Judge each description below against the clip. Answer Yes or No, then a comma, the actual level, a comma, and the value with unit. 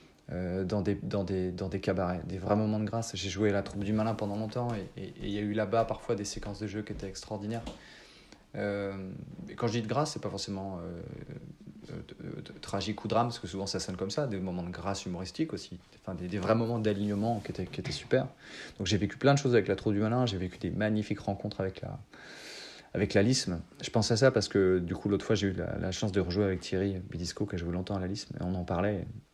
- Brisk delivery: Yes, fast, 260 wpm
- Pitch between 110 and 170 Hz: No, low, 100 Hz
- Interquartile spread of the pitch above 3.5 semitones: No, narrow, 2.5 semitones